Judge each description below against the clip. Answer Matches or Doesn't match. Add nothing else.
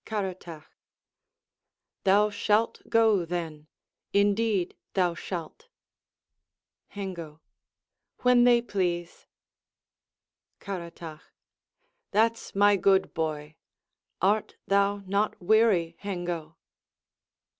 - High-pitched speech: Matches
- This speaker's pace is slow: Matches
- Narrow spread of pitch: Doesn't match